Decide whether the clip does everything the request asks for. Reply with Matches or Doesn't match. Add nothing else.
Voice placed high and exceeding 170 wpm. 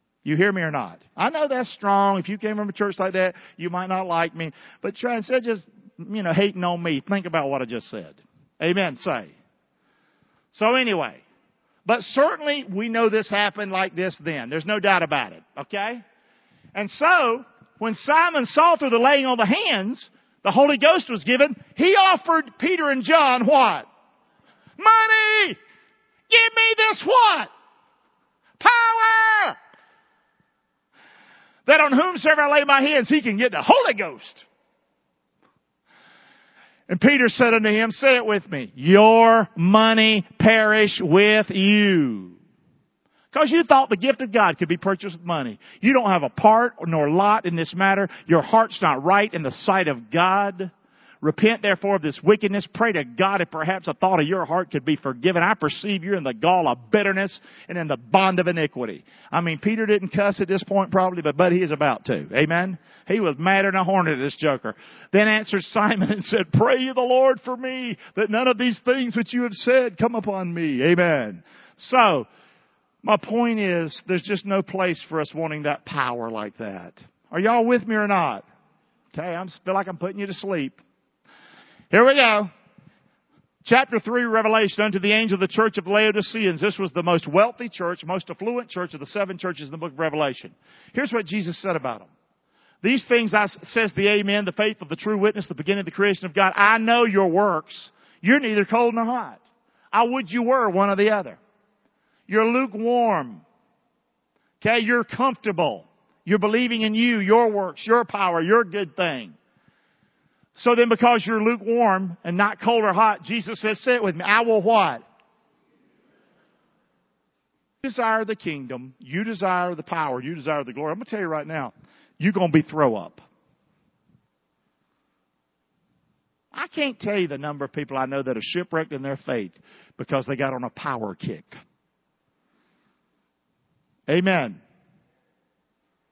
Matches